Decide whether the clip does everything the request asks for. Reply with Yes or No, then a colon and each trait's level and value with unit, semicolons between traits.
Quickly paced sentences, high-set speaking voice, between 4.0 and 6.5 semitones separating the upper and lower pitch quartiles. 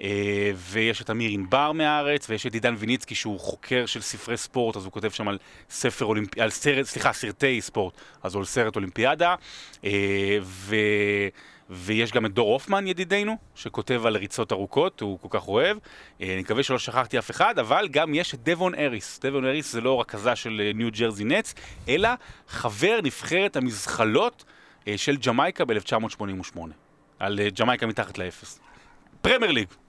No: fast, 175 wpm; low, 110 Hz; average, 4.3 semitones